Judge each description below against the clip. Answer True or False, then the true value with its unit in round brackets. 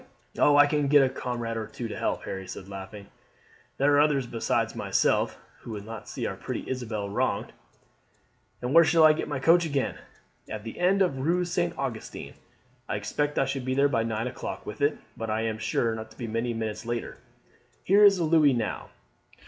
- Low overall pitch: True (130 Hz)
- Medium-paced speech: False (210 wpm)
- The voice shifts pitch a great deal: False (4.8 semitones)